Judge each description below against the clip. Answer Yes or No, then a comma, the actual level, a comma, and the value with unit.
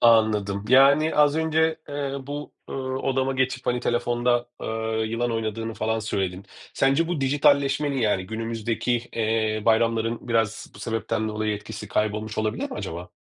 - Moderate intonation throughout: Yes, average, 3.6 semitones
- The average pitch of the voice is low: Yes, low, 115 Hz